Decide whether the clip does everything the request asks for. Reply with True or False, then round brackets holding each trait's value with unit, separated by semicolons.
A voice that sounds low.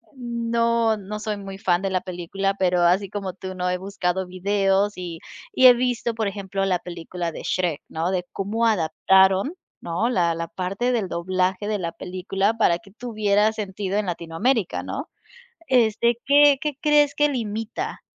False (195 Hz)